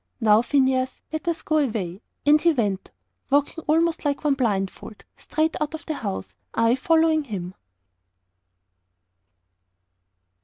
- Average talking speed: No, slow, 125 wpm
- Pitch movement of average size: No, wide, 6.1 semitones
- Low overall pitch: No, very high, 275 Hz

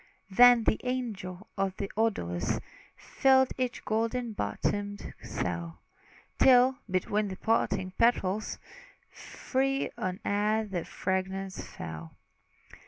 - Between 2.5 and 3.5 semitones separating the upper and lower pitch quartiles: No, average, 4.5 semitones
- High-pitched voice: Yes, high, 205 Hz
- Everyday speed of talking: No, slow, 105 wpm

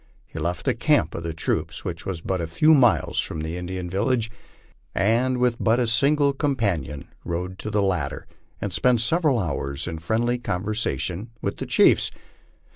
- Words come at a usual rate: Yes, average, 175 wpm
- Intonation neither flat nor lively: No, wide, 6.1 semitones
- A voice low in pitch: Yes, low, 100 Hz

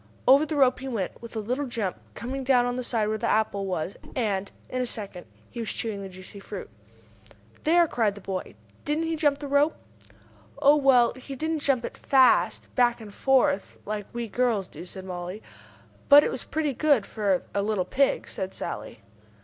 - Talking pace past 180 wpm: Yes, average, 200 wpm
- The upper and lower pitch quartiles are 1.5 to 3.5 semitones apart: No, average, 5.3 semitones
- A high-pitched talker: Yes, high, 235 Hz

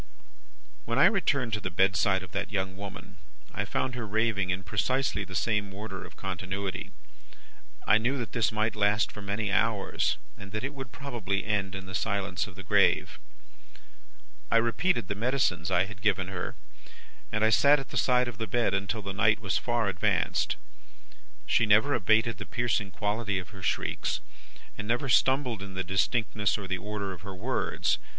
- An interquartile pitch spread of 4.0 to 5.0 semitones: No, average, 3.2 semitones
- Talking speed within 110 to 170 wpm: No, average, 180 wpm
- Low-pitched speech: Yes, low, 105 Hz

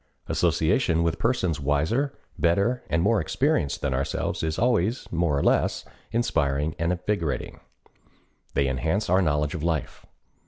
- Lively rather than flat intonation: Yes, wide, 6.2 semitones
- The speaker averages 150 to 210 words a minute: No, slow, 135 wpm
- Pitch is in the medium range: No, very low, 85 Hz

